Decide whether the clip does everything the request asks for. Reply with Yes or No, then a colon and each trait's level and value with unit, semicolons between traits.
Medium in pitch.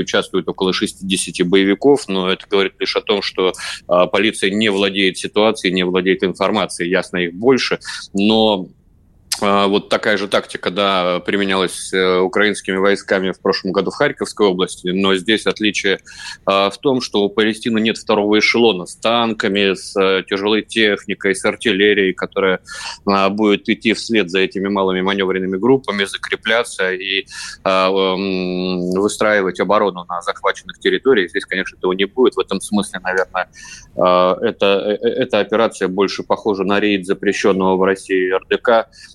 No: low, 100 Hz